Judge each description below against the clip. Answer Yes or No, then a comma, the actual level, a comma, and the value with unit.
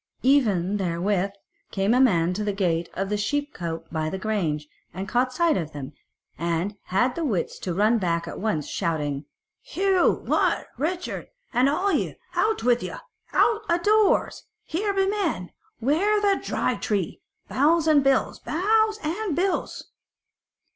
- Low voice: No, high, 230 Hz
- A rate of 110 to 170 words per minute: Yes, average, 160 wpm